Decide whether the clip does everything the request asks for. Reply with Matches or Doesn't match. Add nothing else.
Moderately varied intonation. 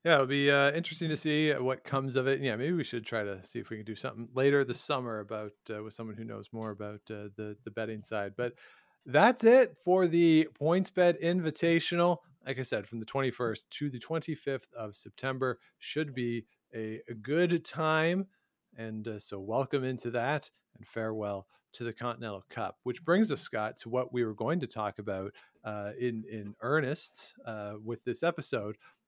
Doesn't match